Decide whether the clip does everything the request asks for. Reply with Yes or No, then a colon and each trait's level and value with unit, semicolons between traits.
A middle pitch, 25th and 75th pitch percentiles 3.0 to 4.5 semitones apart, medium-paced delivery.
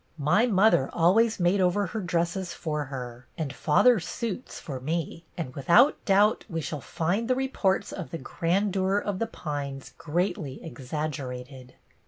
No: medium, 170 Hz; wide, 5.5 semitones; average, 150 wpm